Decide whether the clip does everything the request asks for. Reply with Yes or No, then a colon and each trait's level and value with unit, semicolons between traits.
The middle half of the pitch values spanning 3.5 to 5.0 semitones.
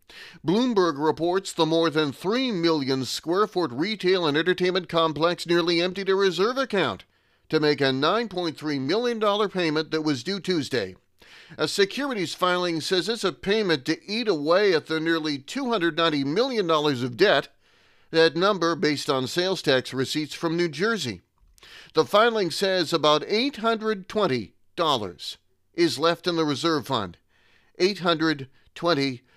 Yes: average, 4.2 semitones